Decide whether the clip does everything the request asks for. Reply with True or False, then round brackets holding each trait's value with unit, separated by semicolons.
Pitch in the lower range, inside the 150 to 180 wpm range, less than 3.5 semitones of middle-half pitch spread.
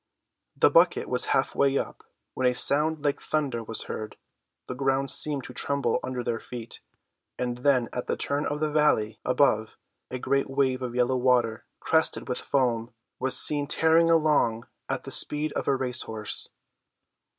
True (130 Hz; 175 wpm; 2.9 semitones)